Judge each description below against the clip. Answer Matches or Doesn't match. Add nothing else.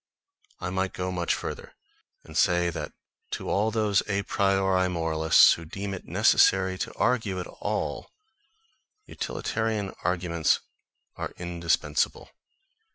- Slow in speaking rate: Matches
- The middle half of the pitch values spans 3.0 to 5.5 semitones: Doesn't match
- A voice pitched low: Matches